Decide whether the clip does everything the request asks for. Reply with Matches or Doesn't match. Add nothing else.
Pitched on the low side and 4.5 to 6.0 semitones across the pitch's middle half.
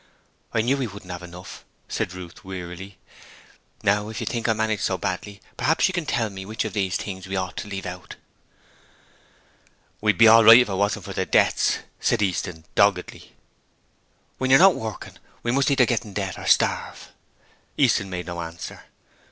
Doesn't match